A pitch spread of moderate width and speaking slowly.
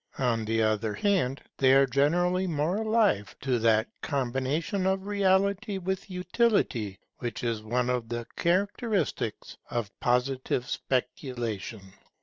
No: wide, 8.3 semitones; slow, 125 wpm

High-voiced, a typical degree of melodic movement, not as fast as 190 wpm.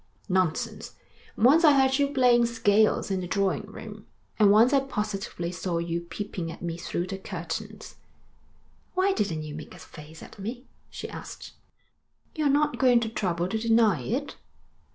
No: high, 210 Hz; wide, 5.7 semitones; average, 165 wpm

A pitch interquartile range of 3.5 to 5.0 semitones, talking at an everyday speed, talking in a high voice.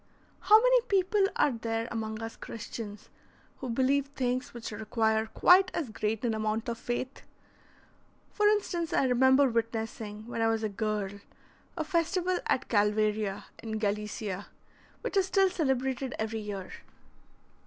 Yes: average, 4.6 semitones; average, 145 wpm; high, 230 Hz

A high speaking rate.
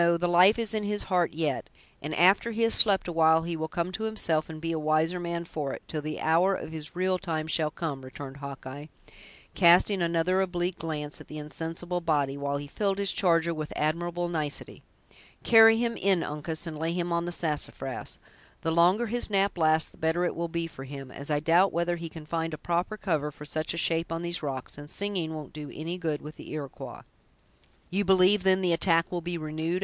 Yes: fast, 215 wpm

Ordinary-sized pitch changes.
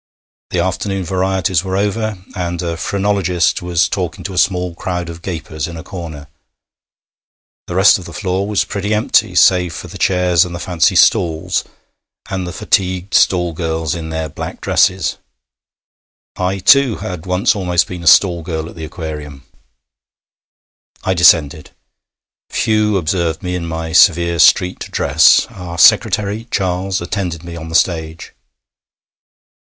No: narrow, 2.3 semitones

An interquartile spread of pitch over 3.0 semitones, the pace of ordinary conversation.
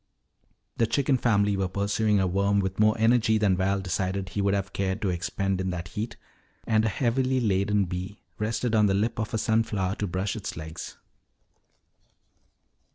No: narrow, 2.5 semitones; average, 175 wpm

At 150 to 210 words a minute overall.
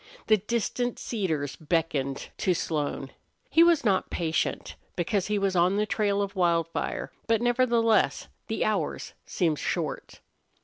No: slow, 135 wpm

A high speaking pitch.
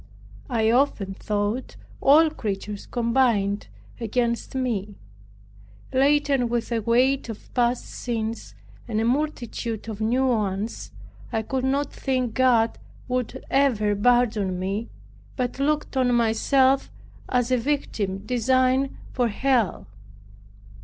Yes: high, 240 Hz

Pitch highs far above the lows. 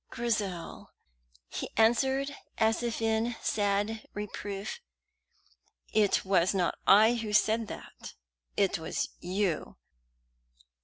No: narrow, 2.4 semitones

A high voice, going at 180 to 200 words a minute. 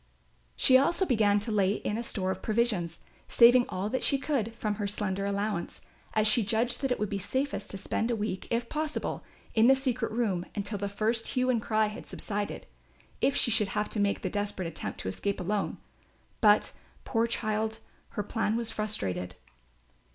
Yes: high, 215 Hz; average, 190 wpm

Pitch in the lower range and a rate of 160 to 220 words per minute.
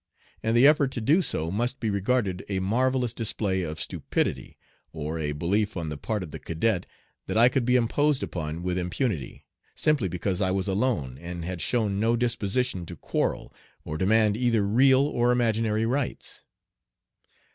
Yes: low, 105 Hz; average, 170 wpm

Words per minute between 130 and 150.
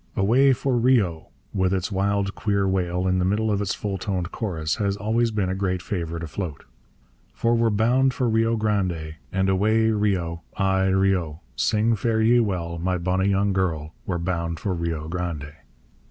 No: average, 175 wpm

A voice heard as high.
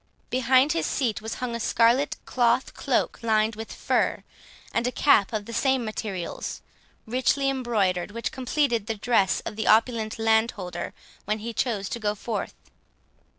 Yes: high, 230 Hz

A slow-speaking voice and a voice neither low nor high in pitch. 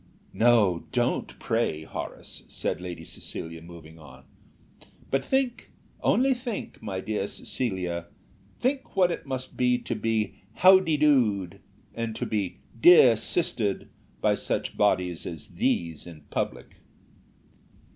No: slow, 130 wpm; low, 110 Hz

